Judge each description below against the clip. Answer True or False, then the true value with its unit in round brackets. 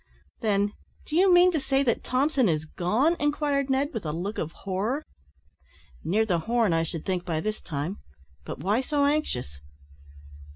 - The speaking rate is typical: True (170 wpm)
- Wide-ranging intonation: True (8.4 semitones)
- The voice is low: False (220 Hz)